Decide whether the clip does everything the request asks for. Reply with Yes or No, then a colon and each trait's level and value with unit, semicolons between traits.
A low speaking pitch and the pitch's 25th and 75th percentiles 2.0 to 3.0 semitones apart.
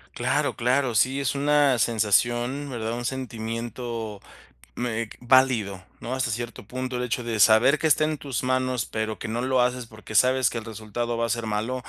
Yes: low, 120 Hz; narrow, 2.5 semitones